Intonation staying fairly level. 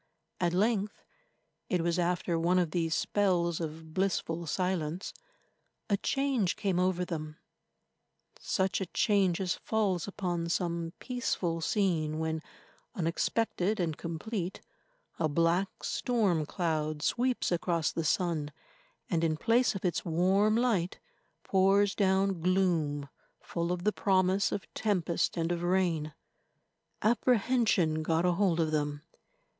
No: average, 3.1 semitones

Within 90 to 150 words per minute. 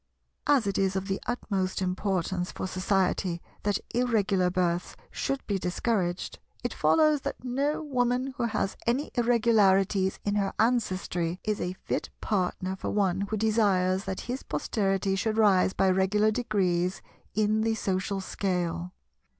Yes: average, 145 wpm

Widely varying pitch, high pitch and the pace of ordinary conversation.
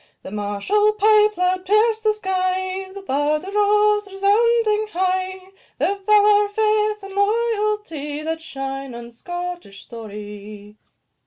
No: wide, 6.0 semitones; very high, 385 Hz; slow, 115 wpm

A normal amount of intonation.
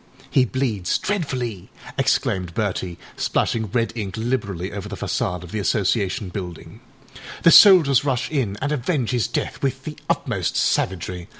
No: wide, 5.8 semitones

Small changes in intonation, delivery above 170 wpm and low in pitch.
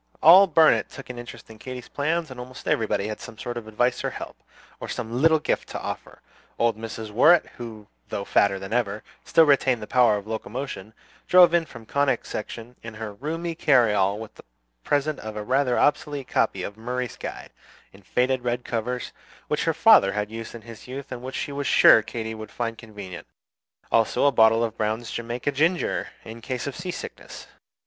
No: average, 3.9 semitones; average, 195 wpm; low, 120 Hz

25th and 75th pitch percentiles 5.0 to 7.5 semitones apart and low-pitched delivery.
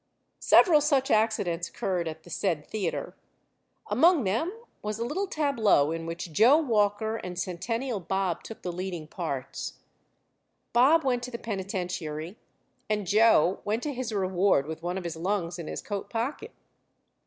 No: average, 5.3 semitones; high, 200 Hz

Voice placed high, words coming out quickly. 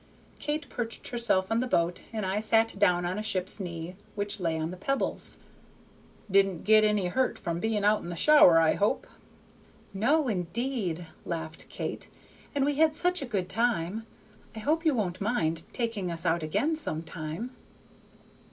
No: high, 205 Hz; average, 170 wpm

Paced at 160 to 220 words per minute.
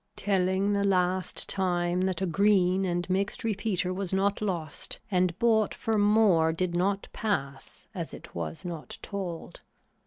No: average, 150 wpm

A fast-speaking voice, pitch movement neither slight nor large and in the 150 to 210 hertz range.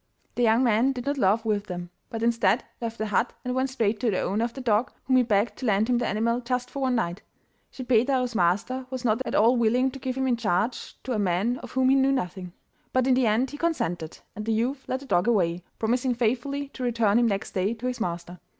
No: fast, 250 wpm; average, 3.4 semitones; high, 235 Hz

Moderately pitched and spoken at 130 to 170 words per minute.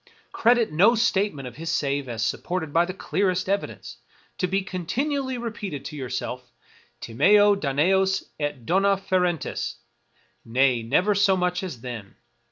Yes: medium, 180 Hz; average, 145 wpm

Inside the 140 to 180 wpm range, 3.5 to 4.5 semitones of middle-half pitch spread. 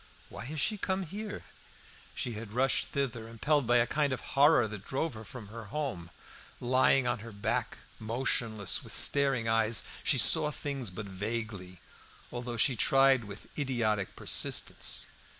Yes: average, 165 wpm; average, 4.0 semitones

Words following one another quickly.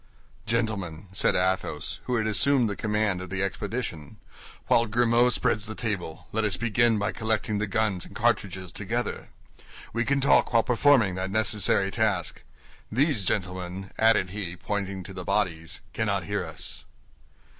No: average, 155 wpm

